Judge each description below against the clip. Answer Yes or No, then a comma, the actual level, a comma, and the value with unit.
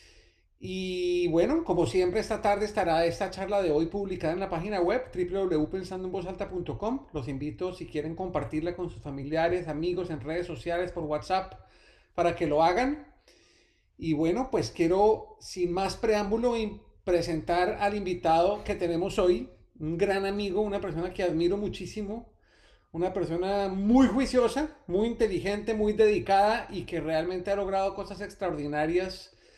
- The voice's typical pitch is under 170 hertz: No, medium, 185 Hz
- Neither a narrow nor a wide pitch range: Yes, average, 3.2 semitones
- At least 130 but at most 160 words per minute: Yes, average, 145 wpm